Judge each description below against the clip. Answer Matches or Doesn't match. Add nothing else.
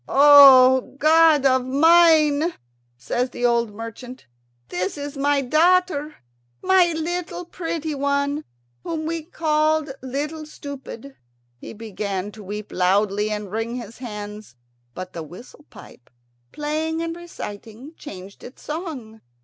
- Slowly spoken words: Matches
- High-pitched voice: Matches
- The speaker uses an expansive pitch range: Matches